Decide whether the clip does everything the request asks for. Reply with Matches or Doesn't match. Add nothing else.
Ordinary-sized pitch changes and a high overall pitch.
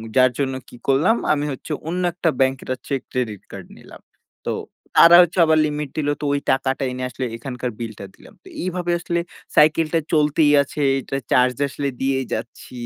Doesn't match